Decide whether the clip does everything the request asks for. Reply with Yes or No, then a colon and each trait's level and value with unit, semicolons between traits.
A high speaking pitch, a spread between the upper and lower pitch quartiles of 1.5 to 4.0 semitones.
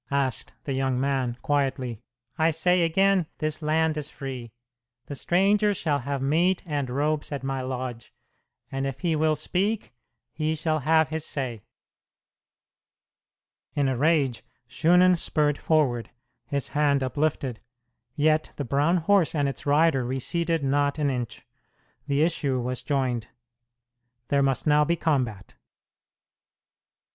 No: medium, 145 Hz; average, 3.1 semitones